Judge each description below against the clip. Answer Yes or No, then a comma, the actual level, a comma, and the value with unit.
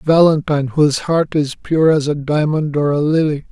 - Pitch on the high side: No, medium, 150 Hz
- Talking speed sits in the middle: Yes, average, 190 wpm